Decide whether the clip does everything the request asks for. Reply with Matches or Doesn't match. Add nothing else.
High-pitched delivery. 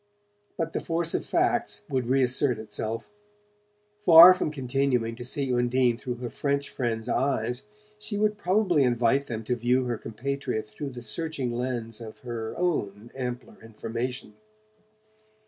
Doesn't match